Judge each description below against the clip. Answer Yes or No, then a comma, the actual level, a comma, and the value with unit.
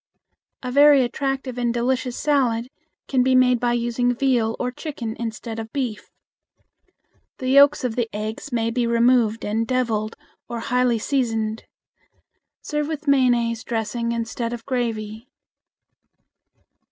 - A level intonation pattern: Yes, narrow, 2.1 semitones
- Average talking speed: No, slow, 130 wpm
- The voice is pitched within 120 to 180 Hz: No, high, 240 Hz